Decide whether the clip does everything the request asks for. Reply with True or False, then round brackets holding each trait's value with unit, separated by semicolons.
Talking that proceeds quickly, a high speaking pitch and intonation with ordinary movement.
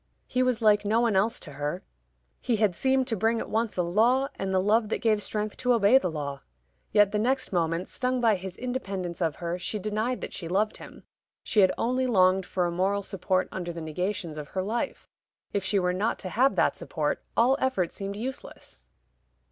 True (210 wpm; 205 Hz; 4.2 semitones)